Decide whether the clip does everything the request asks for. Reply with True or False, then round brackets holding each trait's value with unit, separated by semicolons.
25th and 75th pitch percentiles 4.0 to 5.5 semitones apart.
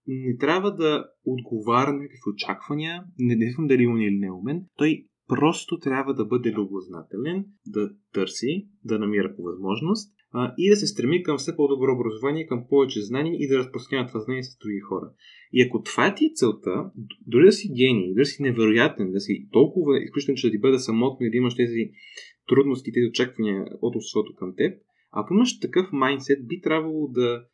True (4.7 semitones)